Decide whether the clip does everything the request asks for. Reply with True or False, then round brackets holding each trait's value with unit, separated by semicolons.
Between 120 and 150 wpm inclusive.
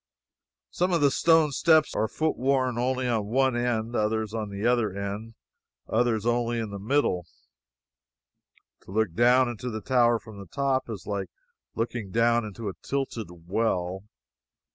False (165 wpm)